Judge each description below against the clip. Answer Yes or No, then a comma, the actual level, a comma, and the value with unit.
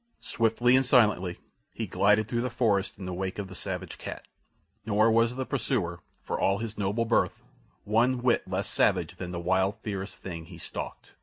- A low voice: Yes, low, 105 Hz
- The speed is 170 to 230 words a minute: Yes, average, 185 wpm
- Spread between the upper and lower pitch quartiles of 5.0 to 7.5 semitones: No, average, 3.7 semitones